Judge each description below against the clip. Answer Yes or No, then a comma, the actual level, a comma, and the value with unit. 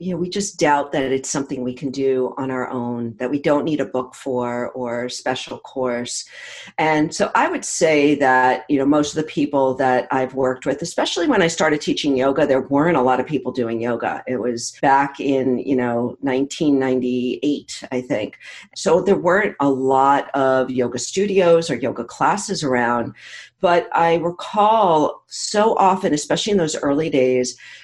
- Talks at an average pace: Yes, average, 185 wpm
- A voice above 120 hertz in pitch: Yes, low, 135 Hz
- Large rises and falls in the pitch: No, average, 3.6 semitones